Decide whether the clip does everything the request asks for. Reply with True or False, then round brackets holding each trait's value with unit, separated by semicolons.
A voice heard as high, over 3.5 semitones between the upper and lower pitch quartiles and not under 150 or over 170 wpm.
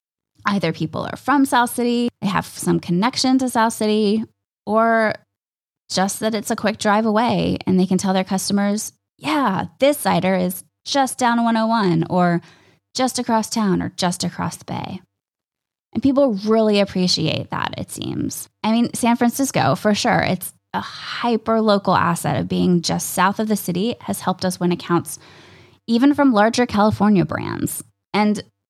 True (205 Hz; 4.4 semitones; 165 wpm)